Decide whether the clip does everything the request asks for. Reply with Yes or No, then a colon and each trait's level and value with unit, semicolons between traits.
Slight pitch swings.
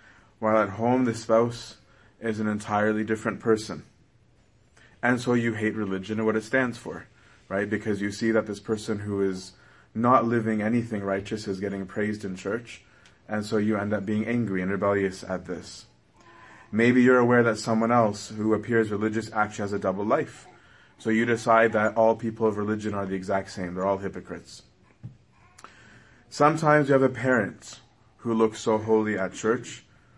Yes: narrow, 2.2 semitones